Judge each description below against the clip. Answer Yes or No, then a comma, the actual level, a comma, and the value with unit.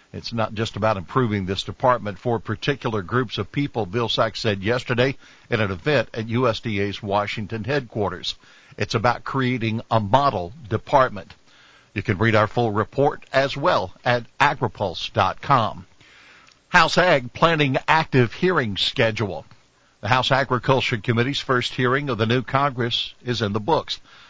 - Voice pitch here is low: Yes, low, 120 Hz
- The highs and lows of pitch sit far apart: No, average, 3.3 semitones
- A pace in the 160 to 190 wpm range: No, average, 145 wpm